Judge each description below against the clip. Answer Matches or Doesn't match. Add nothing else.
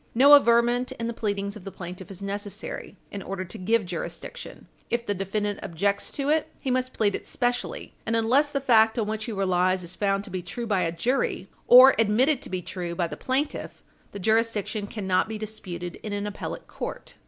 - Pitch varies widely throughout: Doesn't match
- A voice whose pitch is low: Doesn't match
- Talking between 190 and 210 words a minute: Matches